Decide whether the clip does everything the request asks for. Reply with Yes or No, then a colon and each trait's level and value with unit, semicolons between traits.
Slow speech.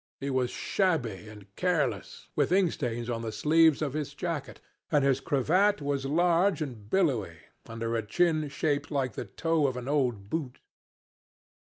No: average, 165 wpm